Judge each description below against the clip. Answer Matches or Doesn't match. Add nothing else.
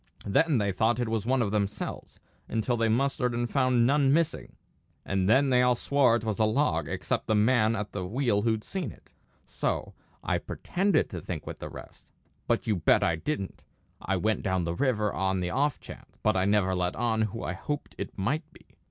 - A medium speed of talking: Doesn't match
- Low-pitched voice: Matches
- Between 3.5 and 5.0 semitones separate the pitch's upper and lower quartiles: Matches